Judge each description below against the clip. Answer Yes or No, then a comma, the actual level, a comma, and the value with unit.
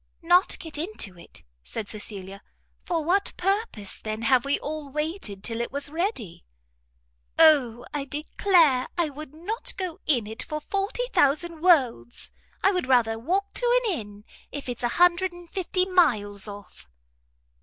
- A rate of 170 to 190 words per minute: No, average, 155 wpm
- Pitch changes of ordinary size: No, wide, 7.8 semitones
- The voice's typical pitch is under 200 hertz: No, very high, 300 Hz